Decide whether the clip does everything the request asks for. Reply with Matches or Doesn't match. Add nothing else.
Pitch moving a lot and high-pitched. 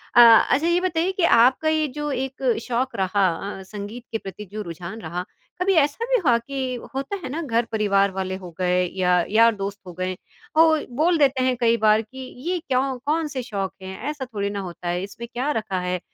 Matches